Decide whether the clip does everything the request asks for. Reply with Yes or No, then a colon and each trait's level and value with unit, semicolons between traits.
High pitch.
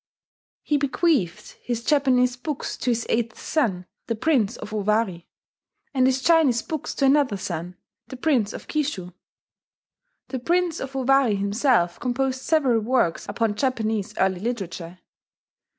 Yes: high, 245 Hz